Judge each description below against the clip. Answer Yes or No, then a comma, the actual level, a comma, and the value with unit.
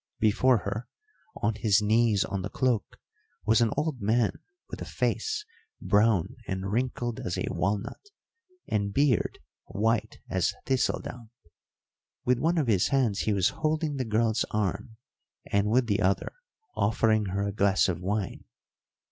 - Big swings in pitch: No, average, 3.6 semitones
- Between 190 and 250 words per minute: No, average, 150 wpm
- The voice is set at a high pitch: No, low, 110 Hz